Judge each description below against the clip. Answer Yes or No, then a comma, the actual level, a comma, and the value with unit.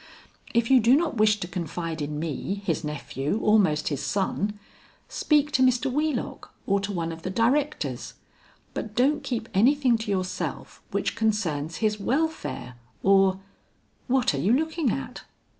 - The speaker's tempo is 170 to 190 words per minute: No, average, 155 wpm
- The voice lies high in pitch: Yes, high, 210 Hz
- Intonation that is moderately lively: No, wide, 6.7 semitones